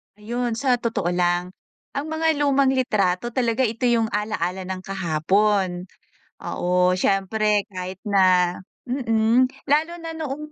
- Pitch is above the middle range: Yes, high, 215 Hz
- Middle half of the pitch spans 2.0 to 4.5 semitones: No, wide, 5.6 semitones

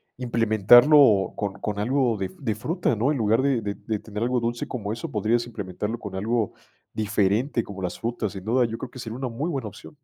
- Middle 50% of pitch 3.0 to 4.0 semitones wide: Yes, average, 3.3 semitones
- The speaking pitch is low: Yes, low, 115 Hz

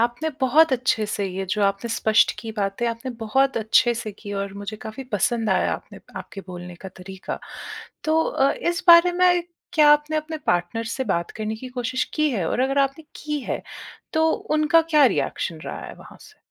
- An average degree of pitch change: No, wide, 6.7 semitones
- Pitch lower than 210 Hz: No, high, 240 Hz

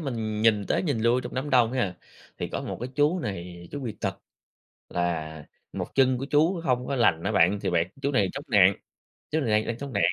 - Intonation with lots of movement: Yes, wide, 5.8 semitones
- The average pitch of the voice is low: Yes, low, 115 Hz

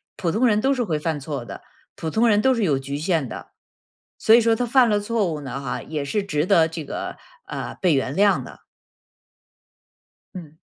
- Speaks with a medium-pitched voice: Yes, medium, 175 Hz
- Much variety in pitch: Yes, wide, 6.7 semitones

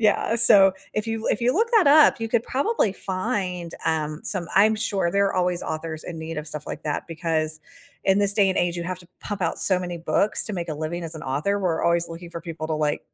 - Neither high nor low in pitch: Yes, medium, 180 Hz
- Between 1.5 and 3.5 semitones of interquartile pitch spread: No, average, 3.9 semitones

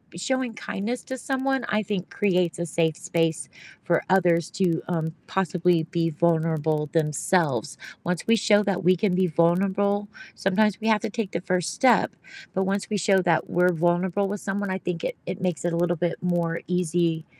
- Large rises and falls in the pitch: No, average, 3.0 semitones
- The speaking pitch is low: No, medium, 180 Hz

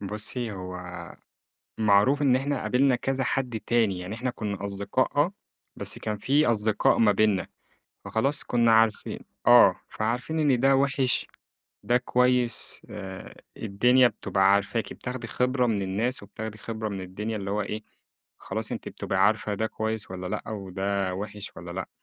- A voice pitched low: Yes, low, 110 Hz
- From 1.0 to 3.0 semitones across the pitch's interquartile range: No, average, 3.8 semitones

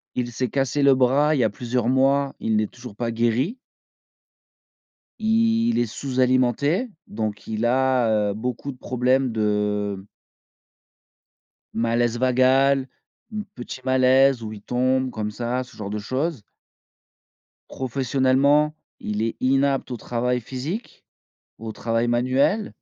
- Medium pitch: No, low, 125 Hz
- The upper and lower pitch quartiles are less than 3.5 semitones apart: Yes, average, 2.9 semitones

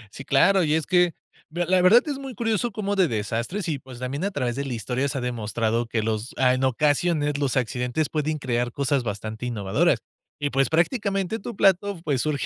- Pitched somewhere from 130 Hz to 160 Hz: Yes, medium, 140 Hz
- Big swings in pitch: Yes, wide, 6.7 semitones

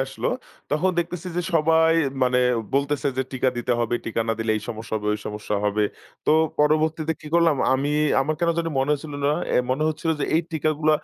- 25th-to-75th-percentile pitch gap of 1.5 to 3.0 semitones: No, average, 4.1 semitones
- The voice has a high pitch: No, medium, 150 Hz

